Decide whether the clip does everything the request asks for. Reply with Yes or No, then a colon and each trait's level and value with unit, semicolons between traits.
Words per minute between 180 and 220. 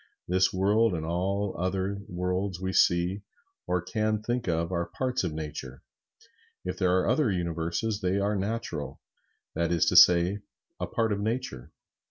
No: average, 160 wpm